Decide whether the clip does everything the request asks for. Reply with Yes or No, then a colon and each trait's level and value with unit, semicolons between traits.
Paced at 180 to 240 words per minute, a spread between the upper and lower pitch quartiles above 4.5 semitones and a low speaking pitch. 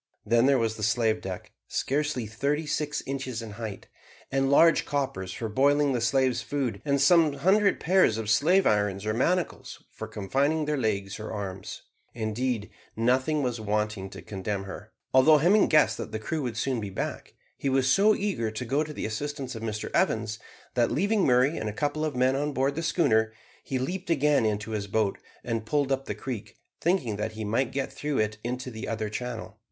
Yes: average, 200 wpm; average, 5.0 semitones; low, 125 Hz